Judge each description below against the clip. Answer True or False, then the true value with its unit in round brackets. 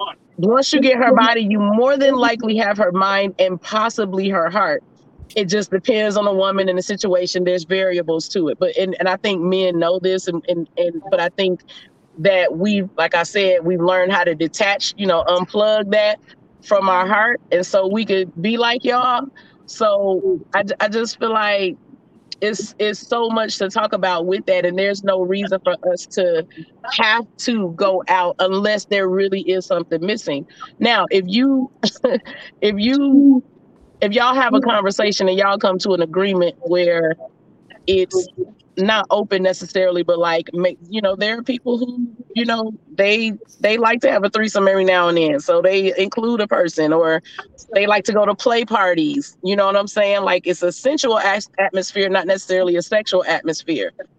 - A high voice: True (195 Hz)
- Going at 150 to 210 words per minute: True (190 wpm)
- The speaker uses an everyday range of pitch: True (3.3 semitones)